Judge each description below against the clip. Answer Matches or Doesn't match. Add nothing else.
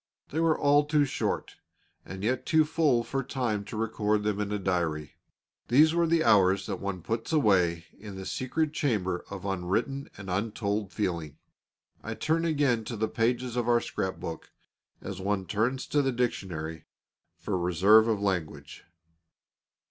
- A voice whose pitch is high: Doesn't match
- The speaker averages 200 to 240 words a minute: Doesn't match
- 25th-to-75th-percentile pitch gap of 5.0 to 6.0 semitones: Matches